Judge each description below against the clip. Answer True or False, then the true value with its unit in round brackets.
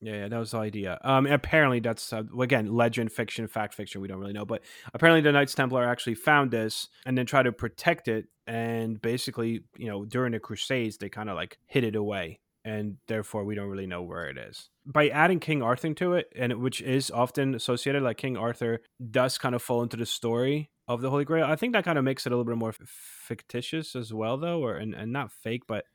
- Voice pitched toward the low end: True (120 Hz)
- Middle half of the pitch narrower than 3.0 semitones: False (3.4 semitones)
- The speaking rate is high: True (240 wpm)